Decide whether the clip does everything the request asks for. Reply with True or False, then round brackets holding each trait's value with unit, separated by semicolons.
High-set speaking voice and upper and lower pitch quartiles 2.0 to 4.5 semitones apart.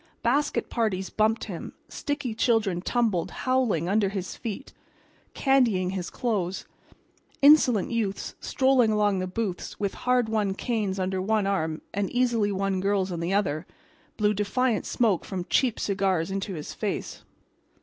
True (205 Hz; 3.7 semitones)